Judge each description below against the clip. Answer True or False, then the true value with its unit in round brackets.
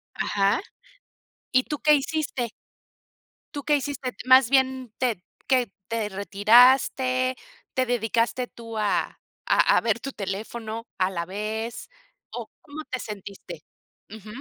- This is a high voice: True (235 Hz)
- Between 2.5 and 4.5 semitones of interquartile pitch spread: True (3.5 semitones)